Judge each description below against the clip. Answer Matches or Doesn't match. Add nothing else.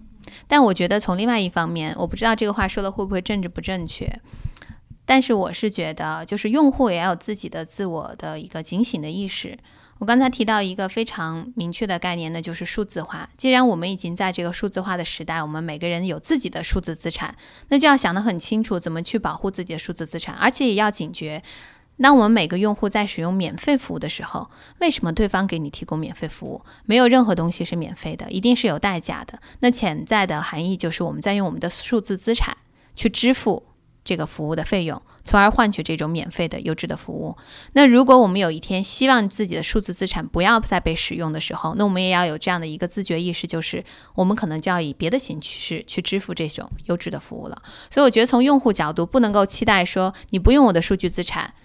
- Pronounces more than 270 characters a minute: Matches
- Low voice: Doesn't match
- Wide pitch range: Doesn't match